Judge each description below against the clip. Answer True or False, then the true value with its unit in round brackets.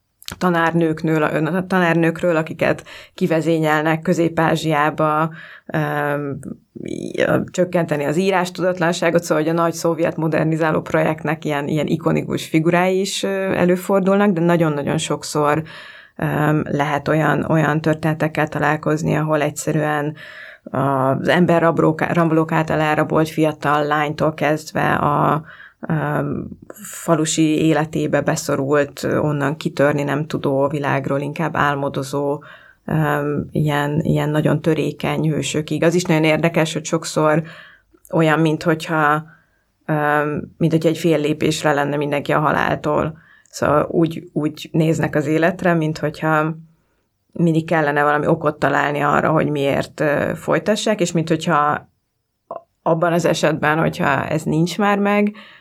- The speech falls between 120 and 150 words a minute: False (105 wpm)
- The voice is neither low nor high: True (155 Hz)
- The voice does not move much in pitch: True (1.9 semitones)